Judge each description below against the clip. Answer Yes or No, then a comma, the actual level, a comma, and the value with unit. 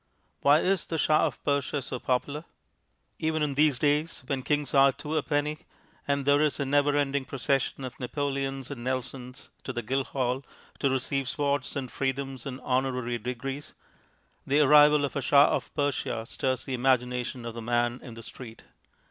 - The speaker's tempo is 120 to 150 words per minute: No, average, 175 wpm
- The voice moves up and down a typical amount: No, narrow, 2.2 semitones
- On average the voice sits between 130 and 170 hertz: Yes, low, 135 Hz